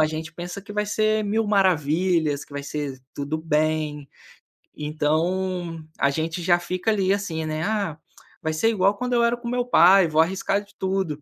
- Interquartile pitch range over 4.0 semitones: Yes, average, 4.4 semitones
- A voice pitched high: No, medium, 175 Hz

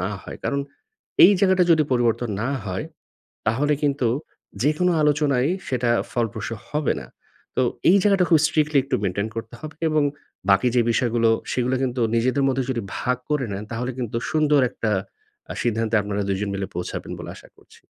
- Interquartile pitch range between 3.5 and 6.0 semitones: Yes, average, 4.6 semitones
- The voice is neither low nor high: No, low, 125 Hz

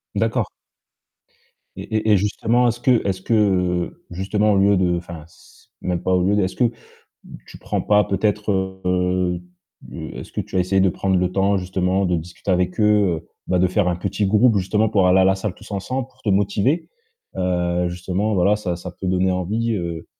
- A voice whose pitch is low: Yes, very low, 95 Hz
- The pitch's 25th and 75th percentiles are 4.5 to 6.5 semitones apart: No, narrow, 2.5 semitones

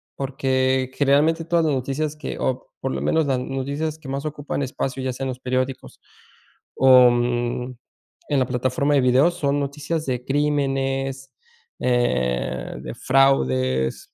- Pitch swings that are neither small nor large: No, narrow, 2.1 semitones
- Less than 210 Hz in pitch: Yes, low, 135 Hz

